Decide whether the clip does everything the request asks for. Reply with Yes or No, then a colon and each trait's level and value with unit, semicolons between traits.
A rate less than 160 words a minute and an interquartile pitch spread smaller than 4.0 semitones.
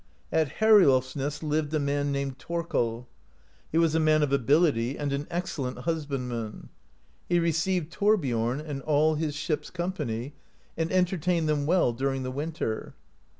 Yes: average, 150 wpm; average, 3.6 semitones